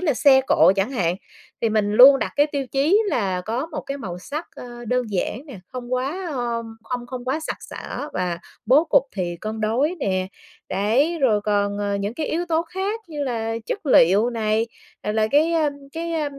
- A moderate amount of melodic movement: No, wide, 5.8 semitones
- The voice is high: Yes, high, 245 Hz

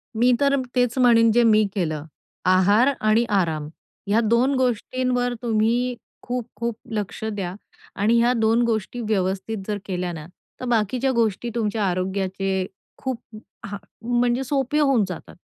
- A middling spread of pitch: Yes, average, 3.8 semitones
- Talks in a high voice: Yes, high, 225 Hz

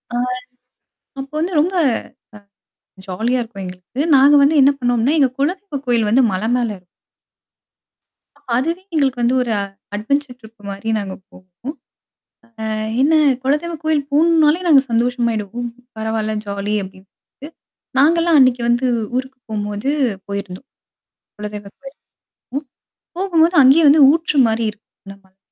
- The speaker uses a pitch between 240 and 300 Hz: Yes, very high, 250 Hz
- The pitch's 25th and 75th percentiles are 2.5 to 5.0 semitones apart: No, wide, 5.6 semitones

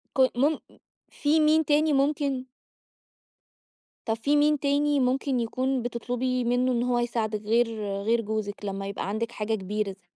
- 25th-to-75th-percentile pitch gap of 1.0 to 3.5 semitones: No, average, 4.1 semitones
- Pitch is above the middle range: Yes, high, 245 Hz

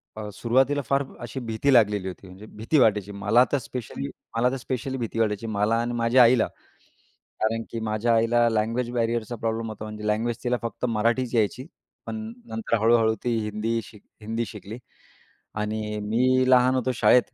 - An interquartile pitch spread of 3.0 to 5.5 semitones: No, narrow, 2.4 semitones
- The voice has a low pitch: Yes, low, 115 Hz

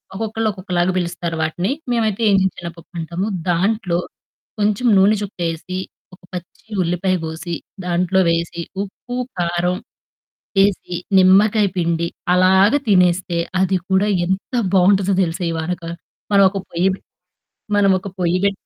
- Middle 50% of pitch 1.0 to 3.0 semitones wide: Yes, narrow, 2.4 semitones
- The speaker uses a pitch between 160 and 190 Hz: Yes, medium, 185 Hz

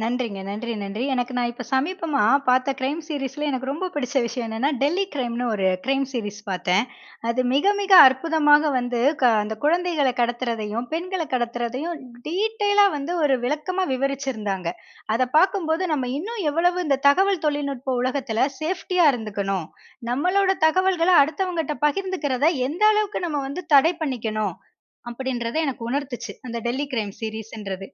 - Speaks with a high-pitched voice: Yes, very high, 270 Hz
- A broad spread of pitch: Yes, wide, 5.8 semitones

